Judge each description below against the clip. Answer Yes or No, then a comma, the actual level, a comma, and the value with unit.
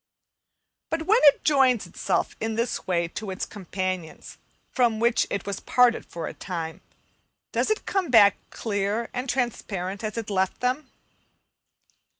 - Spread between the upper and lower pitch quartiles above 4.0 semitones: Yes, average, 4.7 semitones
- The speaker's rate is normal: Yes, average, 150 wpm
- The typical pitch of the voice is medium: No, high, 220 Hz